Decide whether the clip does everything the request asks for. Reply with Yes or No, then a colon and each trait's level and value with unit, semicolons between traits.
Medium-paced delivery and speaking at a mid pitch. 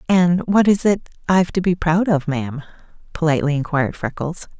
Yes: average, 170 wpm; medium, 165 Hz